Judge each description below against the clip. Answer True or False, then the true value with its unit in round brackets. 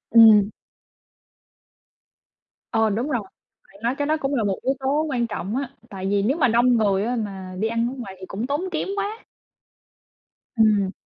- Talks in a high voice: True (230 Hz)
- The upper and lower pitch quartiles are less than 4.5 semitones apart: False (4.8 semitones)